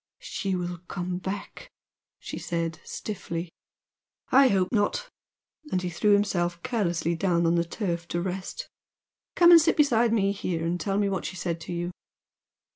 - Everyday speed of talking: Yes, average, 165 wpm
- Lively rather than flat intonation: No, average, 3.1 semitones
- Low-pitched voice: No, medium, 185 Hz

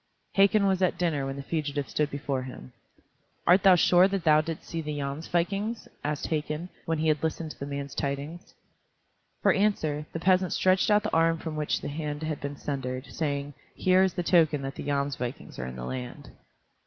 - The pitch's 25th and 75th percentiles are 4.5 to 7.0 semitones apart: No, average, 3.8 semitones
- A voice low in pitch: No, medium, 155 Hz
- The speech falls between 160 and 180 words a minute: No, average, 200 wpm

